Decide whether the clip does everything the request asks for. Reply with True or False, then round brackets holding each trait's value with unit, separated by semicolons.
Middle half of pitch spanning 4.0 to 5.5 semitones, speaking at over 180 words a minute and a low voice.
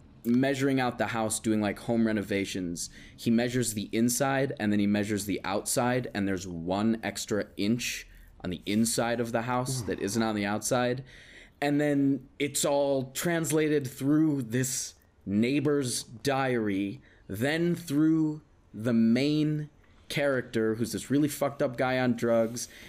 False (4.8 semitones; 145 wpm; 120 Hz)